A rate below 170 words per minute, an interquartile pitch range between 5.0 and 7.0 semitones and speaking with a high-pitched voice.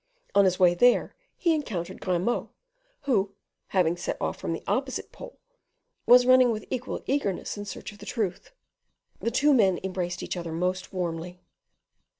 Yes: average, 160 wpm; wide, 5.4 semitones; high, 195 Hz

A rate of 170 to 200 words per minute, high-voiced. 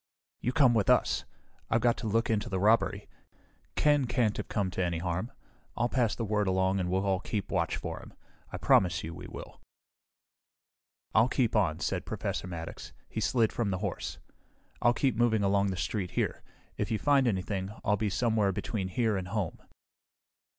No: average, 185 wpm; low, 105 Hz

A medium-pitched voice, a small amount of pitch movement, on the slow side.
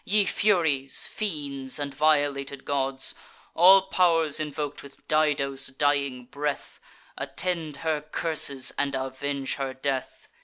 Yes: medium, 145 Hz; narrow, 2.3 semitones; slow, 115 wpm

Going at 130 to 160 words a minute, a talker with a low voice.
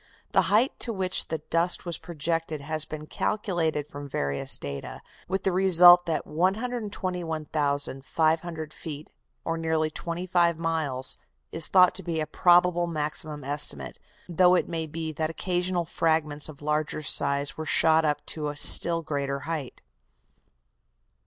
No: average, 140 wpm; medium, 160 Hz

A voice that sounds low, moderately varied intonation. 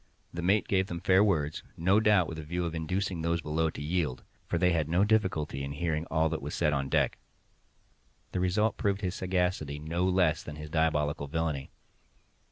Yes: very low, 85 Hz; average, 3.4 semitones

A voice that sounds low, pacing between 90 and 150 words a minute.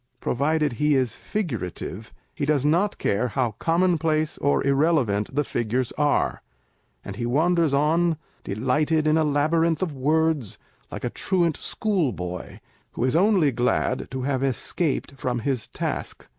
No: medium, 145 Hz; average, 145 wpm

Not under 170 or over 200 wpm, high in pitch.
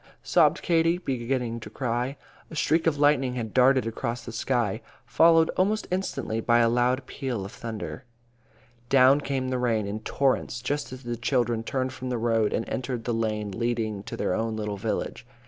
No: average, 180 wpm; low, 125 Hz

